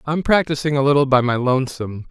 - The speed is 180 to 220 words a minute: Yes, average, 200 wpm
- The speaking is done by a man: Yes, male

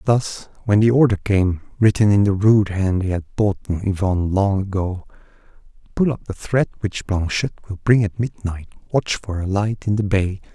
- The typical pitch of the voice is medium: No, low, 100 Hz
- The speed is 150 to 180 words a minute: No, average, 190 wpm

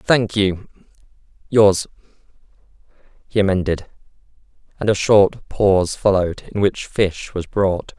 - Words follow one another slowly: Yes, slow, 105 wpm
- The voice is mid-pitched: No, low, 100 Hz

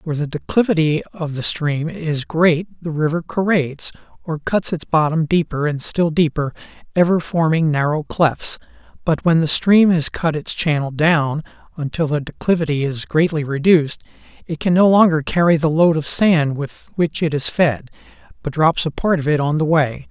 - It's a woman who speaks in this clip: No, male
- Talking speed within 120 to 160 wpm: No, average, 180 wpm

